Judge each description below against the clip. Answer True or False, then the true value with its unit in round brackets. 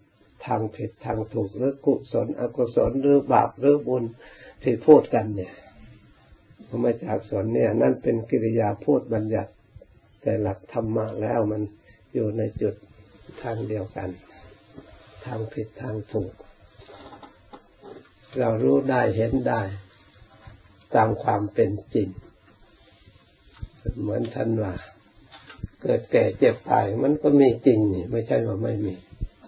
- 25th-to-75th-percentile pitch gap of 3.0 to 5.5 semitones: False (2.6 semitones)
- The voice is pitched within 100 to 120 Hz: True (110 Hz)